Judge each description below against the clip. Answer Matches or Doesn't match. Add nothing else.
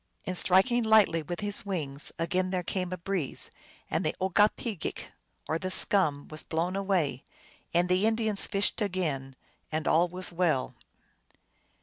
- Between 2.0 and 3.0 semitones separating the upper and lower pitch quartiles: Doesn't match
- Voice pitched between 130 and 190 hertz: Matches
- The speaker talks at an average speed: Matches